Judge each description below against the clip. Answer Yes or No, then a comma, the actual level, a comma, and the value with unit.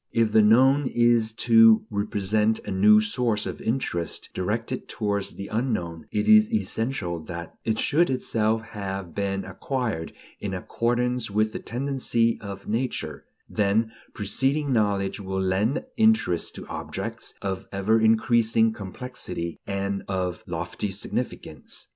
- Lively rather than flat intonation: No, average, 3.4 semitones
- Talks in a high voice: No, low, 110 Hz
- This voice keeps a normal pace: No, slow, 130 wpm